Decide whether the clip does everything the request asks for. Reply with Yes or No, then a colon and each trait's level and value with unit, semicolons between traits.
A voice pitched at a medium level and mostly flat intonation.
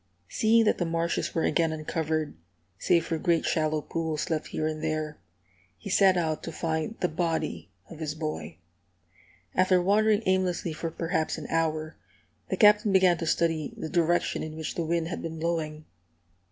Yes: medium, 165 Hz; narrow, 2.0 semitones